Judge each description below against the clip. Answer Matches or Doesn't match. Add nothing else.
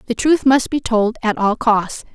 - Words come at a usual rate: Doesn't match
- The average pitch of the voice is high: Matches